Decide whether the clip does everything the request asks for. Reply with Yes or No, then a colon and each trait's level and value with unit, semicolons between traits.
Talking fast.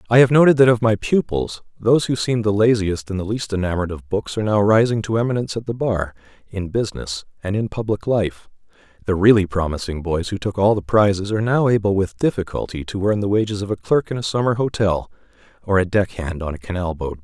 Yes: fast, 225 wpm